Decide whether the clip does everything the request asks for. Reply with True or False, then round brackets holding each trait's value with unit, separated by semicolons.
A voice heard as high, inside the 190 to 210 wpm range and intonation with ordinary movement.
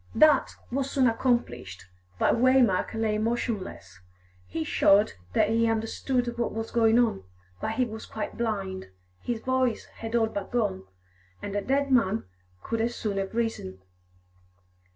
False (225 Hz; 150 wpm; 3.0 semitones)